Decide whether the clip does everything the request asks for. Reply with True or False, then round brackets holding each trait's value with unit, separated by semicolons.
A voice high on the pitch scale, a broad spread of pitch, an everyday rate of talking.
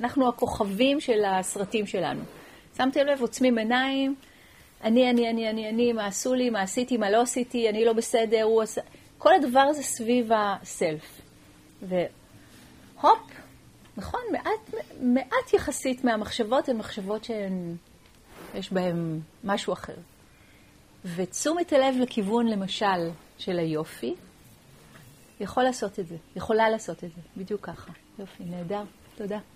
False (225 Hz; 4.4 semitones; 130 wpm)